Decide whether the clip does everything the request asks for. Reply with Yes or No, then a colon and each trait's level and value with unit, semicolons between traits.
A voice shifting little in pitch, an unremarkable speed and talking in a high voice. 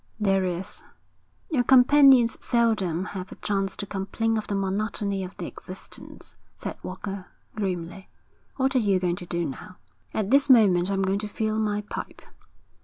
No: average, 3.0 semitones; average, 165 wpm; high, 200 Hz